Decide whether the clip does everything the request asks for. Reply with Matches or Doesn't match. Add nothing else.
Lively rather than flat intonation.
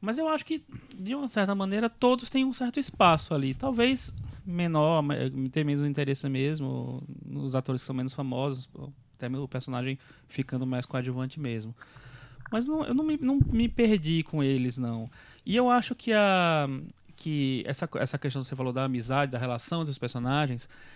Matches